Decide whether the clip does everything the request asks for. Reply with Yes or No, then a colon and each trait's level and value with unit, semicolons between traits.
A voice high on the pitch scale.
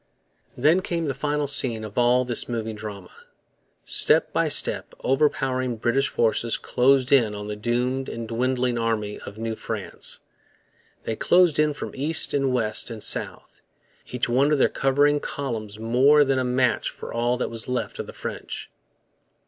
No: low, 125 Hz